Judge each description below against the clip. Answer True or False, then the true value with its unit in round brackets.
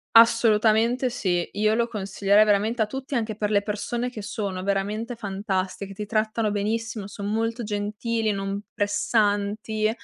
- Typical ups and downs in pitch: False (2.0 semitones)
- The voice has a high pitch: True (215 Hz)